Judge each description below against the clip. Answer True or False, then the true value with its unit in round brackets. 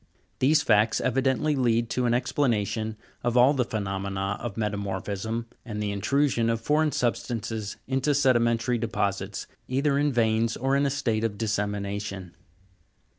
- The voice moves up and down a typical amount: True (4.0 semitones)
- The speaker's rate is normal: True (145 wpm)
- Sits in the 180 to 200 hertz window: False (115 Hz)